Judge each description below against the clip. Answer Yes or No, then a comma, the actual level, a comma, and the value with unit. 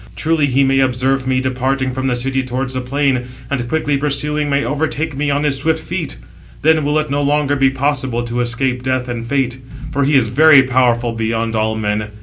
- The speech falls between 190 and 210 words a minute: Yes, fast, 205 wpm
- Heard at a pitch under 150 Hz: Yes, low, 135 Hz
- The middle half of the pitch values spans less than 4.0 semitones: Yes, narrow, 2.6 semitones